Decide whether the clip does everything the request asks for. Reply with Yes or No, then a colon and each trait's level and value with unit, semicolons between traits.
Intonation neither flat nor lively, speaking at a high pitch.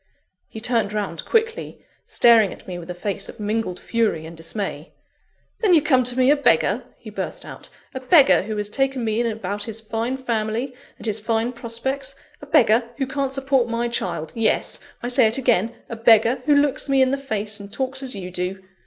Yes: average, 3.9 semitones; high, 230 Hz